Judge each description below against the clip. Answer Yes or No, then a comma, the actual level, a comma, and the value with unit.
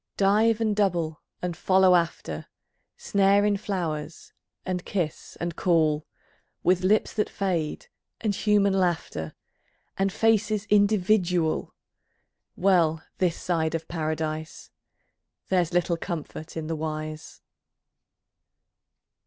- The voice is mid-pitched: Yes, medium, 175 Hz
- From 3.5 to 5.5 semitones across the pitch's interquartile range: Yes, average, 3.8 semitones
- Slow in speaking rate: Yes, slow, 105 wpm